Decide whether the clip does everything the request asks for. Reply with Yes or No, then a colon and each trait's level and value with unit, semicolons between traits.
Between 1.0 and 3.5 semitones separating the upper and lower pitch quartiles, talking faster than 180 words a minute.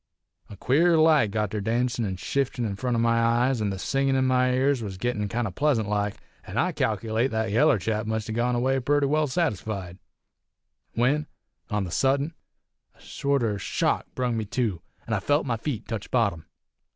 No: average, 4.2 semitones; average, 190 wpm